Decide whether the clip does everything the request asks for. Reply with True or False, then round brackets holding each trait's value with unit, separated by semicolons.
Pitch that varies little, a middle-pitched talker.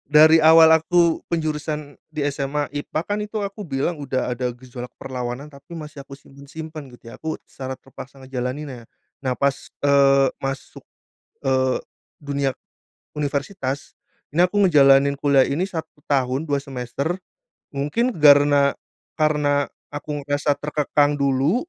True (2.1 semitones; 145 Hz)